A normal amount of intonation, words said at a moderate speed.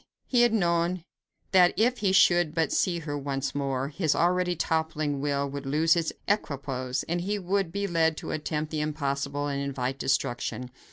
Yes: average, 4.0 semitones; average, 175 wpm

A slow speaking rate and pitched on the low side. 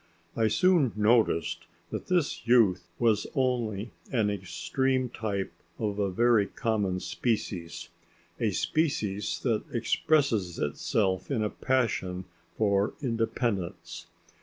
Yes: slow, 110 wpm; low, 110 Hz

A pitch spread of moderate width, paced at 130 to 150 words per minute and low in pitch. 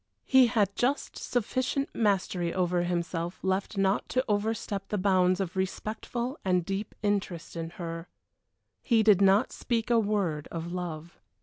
No: average, 3.7 semitones; average, 145 wpm; high, 195 Hz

